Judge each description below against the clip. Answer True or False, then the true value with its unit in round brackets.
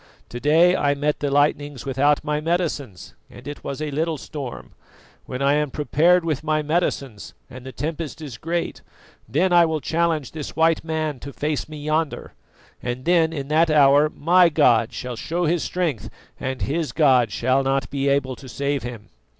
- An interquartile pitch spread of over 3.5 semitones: False (3.0 semitones)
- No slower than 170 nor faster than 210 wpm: True (185 wpm)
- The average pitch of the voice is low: False (150 Hz)